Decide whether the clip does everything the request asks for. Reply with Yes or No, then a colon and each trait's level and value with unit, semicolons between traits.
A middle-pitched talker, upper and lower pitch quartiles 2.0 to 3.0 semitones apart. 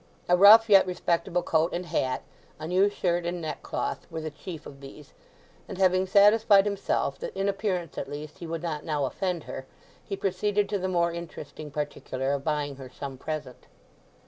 No: medium, 170 Hz; average, 4.4 semitones